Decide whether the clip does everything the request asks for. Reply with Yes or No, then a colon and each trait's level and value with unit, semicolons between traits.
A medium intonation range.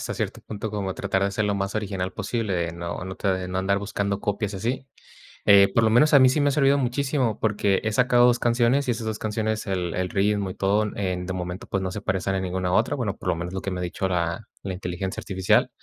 Yes: average, 3.2 semitones